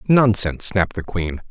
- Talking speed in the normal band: Yes, average, 160 wpm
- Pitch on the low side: Yes, low, 100 Hz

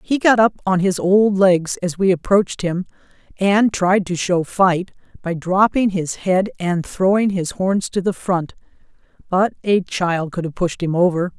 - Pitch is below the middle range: No, medium, 185 Hz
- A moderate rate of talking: Yes, average, 185 wpm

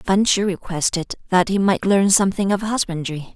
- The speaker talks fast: No, average, 180 wpm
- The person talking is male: No, female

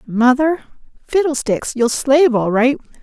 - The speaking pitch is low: No, very high, 265 Hz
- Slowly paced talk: Yes, slow, 120 wpm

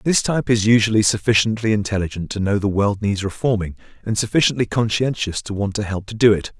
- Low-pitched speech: Yes, low, 105 Hz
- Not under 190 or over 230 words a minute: Yes, average, 200 wpm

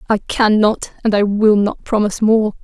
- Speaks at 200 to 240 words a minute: Yes, fast, 205 wpm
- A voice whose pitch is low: No, high, 210 Hz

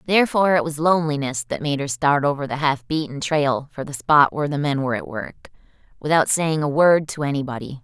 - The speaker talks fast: Yes, fast, 215 wpm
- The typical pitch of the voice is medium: Yes, medium, 145 Hz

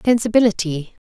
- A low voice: No, high, 205 Hz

